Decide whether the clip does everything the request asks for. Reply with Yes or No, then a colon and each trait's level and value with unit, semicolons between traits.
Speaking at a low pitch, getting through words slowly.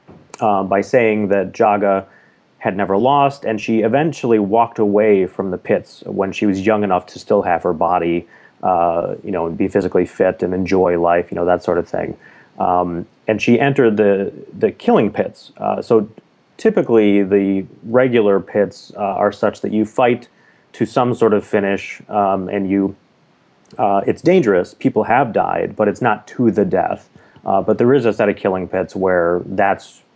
No: low, 100 Hz; average, 185 wpm